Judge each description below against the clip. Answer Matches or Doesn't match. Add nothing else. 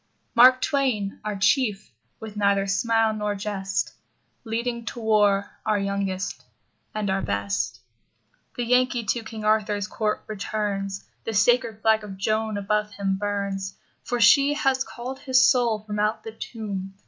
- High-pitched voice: Matches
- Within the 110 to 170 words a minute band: Matches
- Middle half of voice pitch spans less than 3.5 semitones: Matches